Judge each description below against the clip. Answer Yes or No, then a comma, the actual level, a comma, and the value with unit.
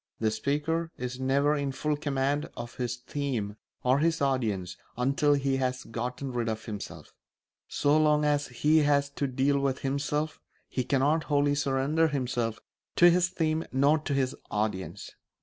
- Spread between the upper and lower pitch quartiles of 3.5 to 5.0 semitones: No, average, 2.8 semitones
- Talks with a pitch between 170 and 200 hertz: No, medium, 140 Hz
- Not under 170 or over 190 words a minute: No, average, 160 wpm